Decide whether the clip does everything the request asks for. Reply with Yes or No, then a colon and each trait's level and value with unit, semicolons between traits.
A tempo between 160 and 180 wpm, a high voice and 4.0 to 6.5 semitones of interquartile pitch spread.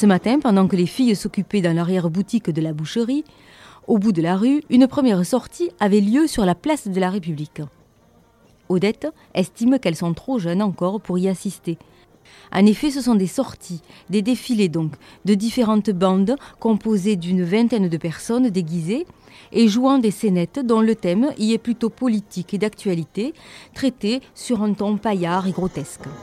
Yes: average, 175 wpm; high, 210 Hz; average, 4.4 semitones